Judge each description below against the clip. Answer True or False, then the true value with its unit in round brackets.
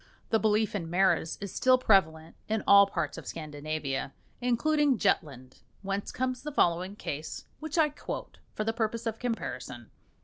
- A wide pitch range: True (6.9 semitones)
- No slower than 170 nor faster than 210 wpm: False (160 wpm)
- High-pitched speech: True (205 Hz)